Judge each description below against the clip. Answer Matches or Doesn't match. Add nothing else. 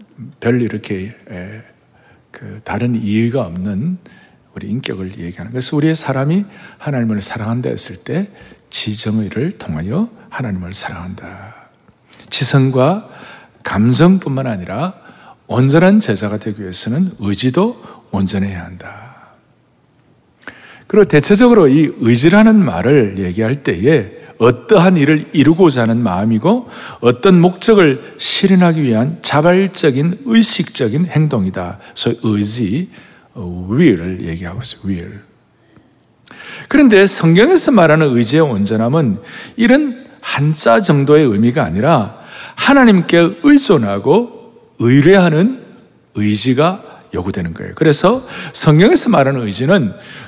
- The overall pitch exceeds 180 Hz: Doesn't match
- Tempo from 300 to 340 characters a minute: Doesn't match